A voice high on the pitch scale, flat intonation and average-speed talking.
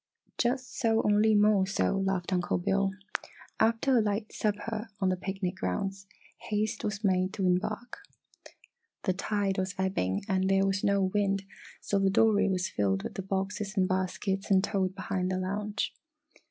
Yes: high, 195 Hz; narrow, 1.9 semitones; average, 165 wpm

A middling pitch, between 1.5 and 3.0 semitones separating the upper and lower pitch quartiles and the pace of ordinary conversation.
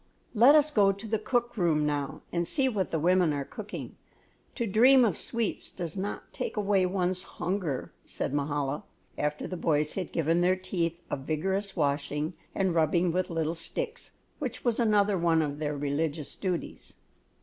No: medium, 180 Hz; average, 5.0 semitones; average, 170 wpm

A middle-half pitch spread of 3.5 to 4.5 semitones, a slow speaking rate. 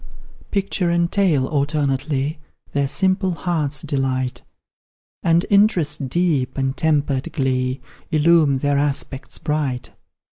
Yes: average, 4.0 semitones; slow, 105 wpm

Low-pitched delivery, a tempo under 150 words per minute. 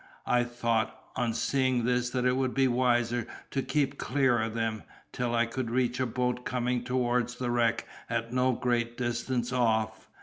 No: low, 120 Hz; average, 175 wpm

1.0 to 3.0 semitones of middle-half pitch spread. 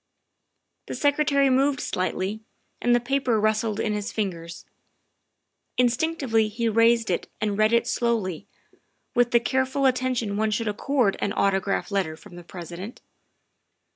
No: average, 3.9 semitones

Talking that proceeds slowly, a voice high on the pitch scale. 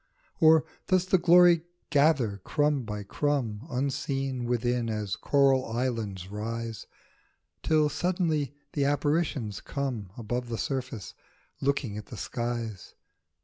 No: slow, 115 wpm; low, 130 Hz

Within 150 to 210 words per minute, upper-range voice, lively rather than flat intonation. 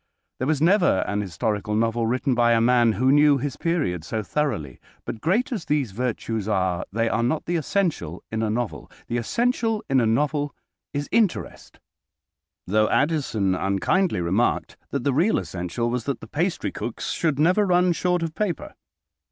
No: average, 170 wpm; low, 125 Hz; wide, 7.1 semitones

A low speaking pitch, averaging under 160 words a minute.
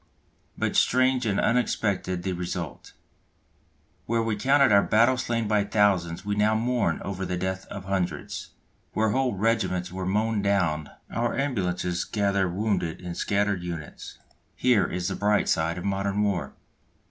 Yes: low, 100 Hz; average, 150 wpm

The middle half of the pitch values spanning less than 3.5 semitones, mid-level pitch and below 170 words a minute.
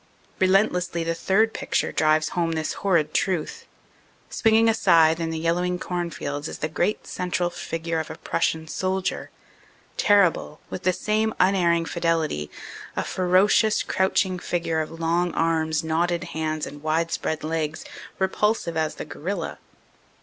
Yes: average, 2.7 semitones; medium, 170 Hz; average, 140 wpm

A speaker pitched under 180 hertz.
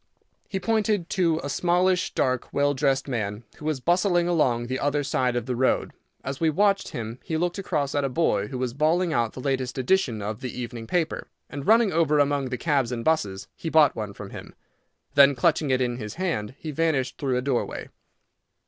Yes: medium, 140 Hz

